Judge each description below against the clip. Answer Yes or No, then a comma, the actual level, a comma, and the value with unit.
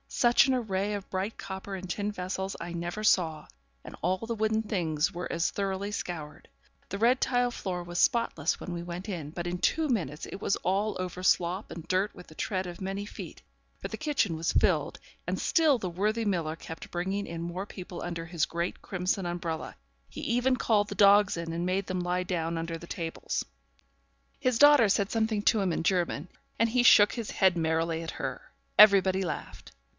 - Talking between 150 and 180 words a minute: No, average, 200 wpm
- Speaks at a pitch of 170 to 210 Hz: Yes, medium, 185 Hz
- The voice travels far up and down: No, average, 3.4 semitones